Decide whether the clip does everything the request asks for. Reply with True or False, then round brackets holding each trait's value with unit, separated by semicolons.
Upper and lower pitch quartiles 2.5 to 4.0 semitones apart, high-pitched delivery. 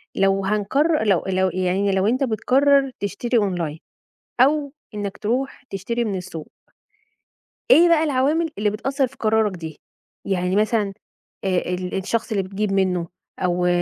False (5.3 semitones; 205 Hz)